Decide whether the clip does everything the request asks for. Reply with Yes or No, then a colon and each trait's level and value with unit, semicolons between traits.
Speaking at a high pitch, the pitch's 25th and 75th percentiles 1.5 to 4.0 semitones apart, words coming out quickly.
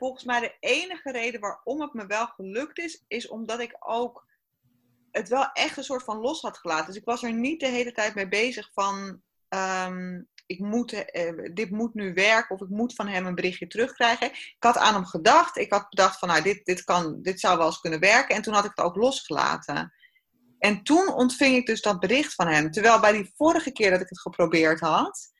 No: high, 215 Hz; average, 4.7 semitones; fast, 225 wpm